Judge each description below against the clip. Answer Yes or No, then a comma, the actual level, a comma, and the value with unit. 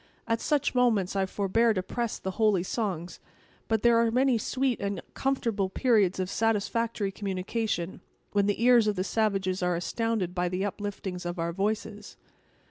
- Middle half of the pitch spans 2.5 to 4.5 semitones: Yes, average, 3.5 semitones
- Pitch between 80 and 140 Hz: No, high, 205 Hz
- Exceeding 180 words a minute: No, average, 165 wpm